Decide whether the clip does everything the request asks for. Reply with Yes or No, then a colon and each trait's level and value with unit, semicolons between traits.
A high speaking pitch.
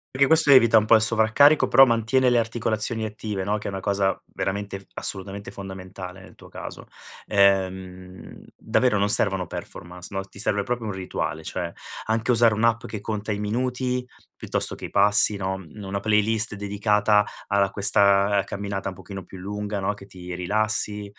No: low, 105 Hz